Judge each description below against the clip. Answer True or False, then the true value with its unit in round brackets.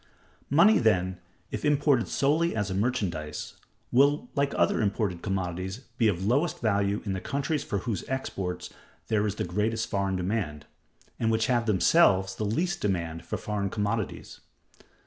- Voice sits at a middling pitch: False (105 Hz)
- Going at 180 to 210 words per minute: False (155 wpm)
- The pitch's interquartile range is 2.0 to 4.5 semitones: False (5.1 semitones)